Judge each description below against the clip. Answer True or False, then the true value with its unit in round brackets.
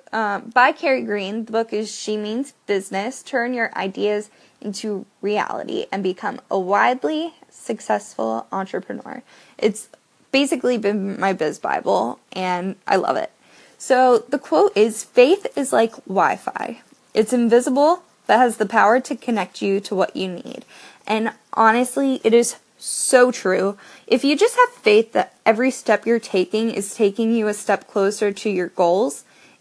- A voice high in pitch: True (220 Hz)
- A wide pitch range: False (4.1 semitones)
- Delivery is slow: False (160 wpm)